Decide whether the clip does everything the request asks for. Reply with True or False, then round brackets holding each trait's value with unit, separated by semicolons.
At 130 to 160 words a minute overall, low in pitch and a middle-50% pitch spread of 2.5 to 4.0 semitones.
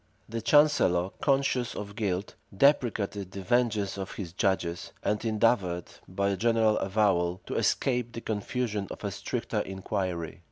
True (145 wpm; 105 Hz; 3.5 semitones)